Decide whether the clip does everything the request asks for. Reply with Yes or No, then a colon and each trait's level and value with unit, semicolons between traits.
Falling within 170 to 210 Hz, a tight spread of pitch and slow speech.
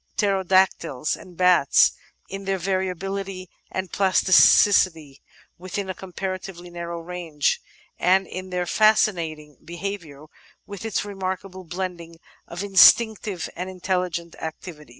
Yes: medium, 185 Hz; narrow, 2.2 semitones; slow, 110 wpm